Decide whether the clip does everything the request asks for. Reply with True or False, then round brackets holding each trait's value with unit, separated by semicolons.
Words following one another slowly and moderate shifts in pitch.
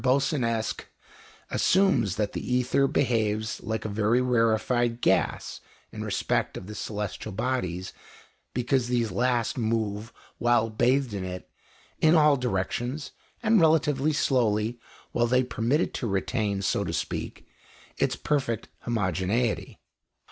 True (125 wpm; 3.2 semitones)